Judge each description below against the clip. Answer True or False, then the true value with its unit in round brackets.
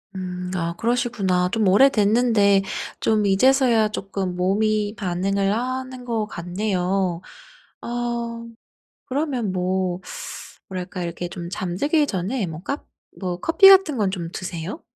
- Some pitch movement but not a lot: True (4.7 semitones)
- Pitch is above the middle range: True (200 Hz)